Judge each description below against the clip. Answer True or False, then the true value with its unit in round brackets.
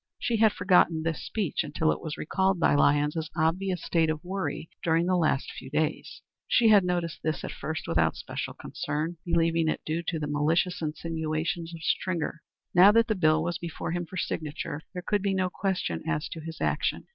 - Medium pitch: True (165 Hz)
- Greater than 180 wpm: True (195 wpm)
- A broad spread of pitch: False (2.5 semitones)